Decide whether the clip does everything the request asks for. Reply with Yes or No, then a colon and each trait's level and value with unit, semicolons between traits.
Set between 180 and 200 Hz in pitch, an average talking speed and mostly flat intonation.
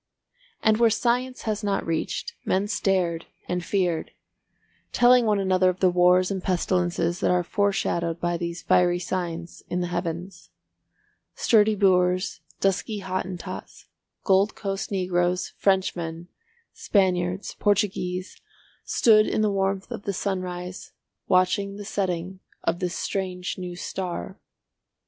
No: medium, 185 Hz; slow, 125 wpm; narrow, 2.0 semitones